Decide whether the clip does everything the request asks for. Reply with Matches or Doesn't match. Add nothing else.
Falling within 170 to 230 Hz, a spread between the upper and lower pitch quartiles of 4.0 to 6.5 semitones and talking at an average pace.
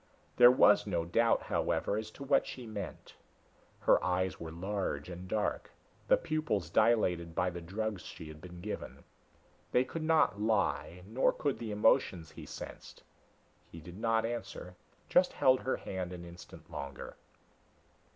Doesn't match